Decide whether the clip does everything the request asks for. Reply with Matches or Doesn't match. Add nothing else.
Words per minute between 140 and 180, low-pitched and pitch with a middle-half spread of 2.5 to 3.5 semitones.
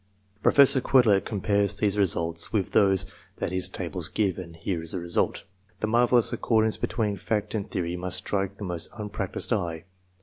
Matches